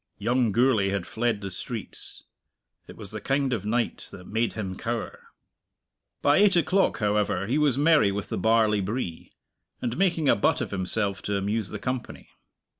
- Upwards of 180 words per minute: No, average, 175 wpm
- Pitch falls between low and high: No, low, 110 Hz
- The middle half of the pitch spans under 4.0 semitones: No, average, 4.3 semitones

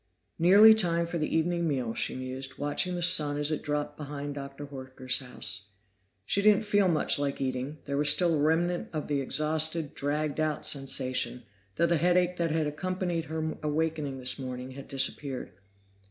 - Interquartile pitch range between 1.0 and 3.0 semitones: No, average, 3.6 semitones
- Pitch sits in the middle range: Yes, medium, 150 Hz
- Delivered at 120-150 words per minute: No, average, 175 wpm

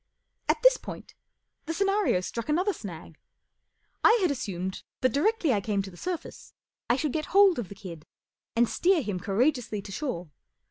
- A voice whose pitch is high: Yes, high, 245 Hz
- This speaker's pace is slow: No, average, 175 wpm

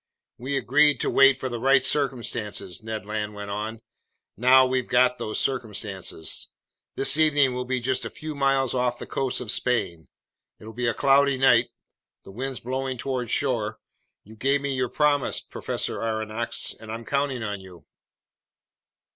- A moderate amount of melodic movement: Yes, average, 3.6 semitones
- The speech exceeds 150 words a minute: Yes, average, 160 wpm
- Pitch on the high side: No, low, 125 Hz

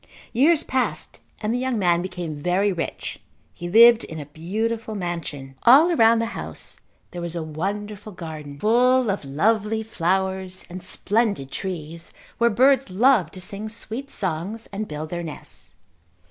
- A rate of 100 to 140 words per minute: No, average, 155 wpm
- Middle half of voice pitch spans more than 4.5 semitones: Yes, average, 5.1 semitones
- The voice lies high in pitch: Yes, high, 195 Hz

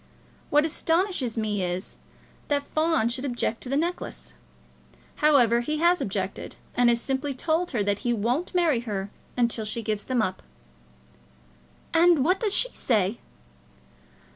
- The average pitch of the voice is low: No, very high, 255 Hz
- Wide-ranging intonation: Yes, wide, 6.2 semitones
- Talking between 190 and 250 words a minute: No, average, 145 wpm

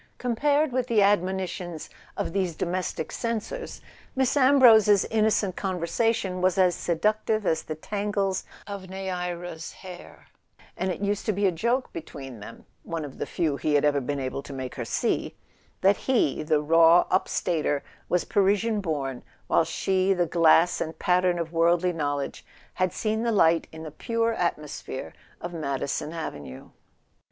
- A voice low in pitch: No, medium, 180 Hz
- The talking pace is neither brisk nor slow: Yes, average, 160 wpm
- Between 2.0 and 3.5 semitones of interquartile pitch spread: No, average, 4.4 semitones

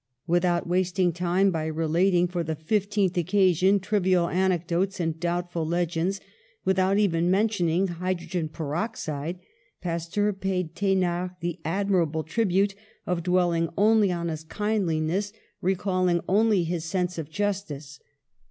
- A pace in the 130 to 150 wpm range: Yes, slow, 135 wpm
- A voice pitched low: No, medium, 180 Hz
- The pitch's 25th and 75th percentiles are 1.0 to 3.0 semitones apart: Yes, narrow, 2.4 semitones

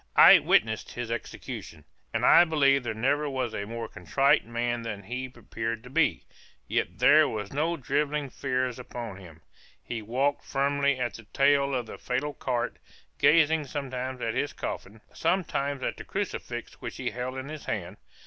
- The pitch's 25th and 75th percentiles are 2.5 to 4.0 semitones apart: Yes, average, 3.3 semitones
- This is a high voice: No, low, 130 Hz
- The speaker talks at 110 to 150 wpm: No, average, 170 wpm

